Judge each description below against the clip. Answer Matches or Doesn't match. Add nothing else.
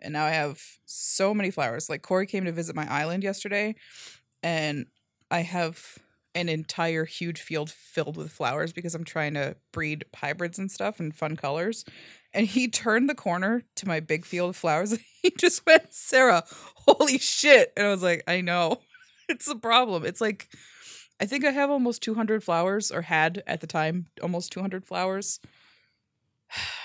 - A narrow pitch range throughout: Doesn't match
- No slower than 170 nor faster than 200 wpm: Matches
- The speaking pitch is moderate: Matches